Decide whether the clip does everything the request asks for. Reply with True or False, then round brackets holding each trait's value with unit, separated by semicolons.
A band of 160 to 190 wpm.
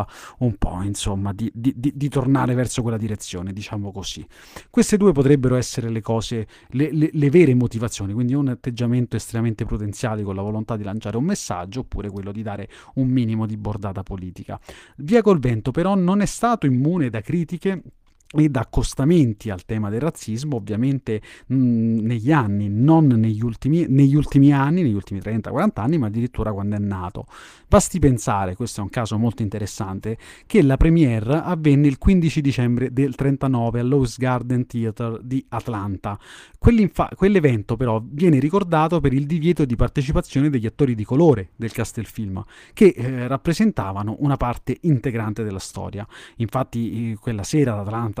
True (165 wpm)